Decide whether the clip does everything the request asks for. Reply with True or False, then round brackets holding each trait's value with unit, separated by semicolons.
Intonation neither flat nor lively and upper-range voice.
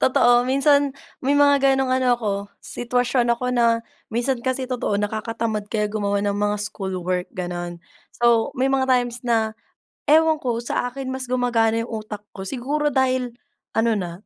True (3.4 semitones; 240 Hz)